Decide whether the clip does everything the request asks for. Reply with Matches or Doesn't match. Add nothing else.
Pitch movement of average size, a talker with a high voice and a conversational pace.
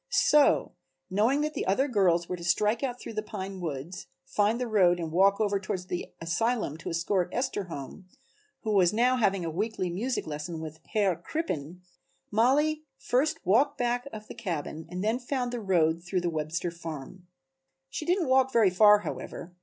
Doesn't match